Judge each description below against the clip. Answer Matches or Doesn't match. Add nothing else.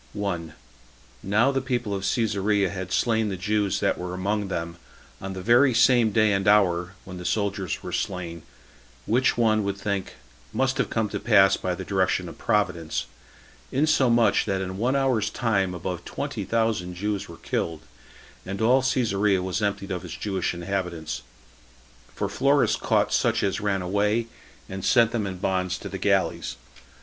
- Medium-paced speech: Matches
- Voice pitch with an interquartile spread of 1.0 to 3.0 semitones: Doesn't match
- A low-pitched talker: Matches